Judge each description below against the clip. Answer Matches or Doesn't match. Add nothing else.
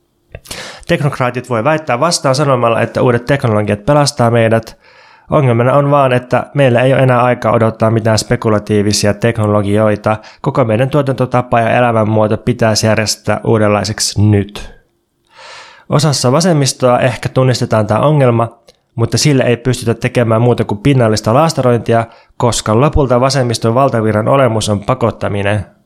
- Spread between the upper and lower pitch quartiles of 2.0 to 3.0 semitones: Doesn't match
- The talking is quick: Doesn't match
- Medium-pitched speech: Doesn't match